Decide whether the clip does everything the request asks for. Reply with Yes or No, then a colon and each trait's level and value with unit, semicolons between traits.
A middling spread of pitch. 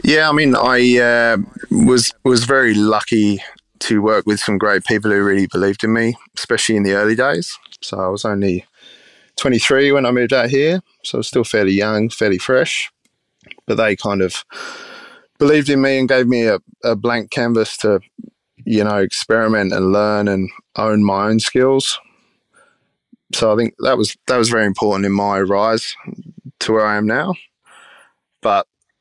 Yes: average, 3.7 semitones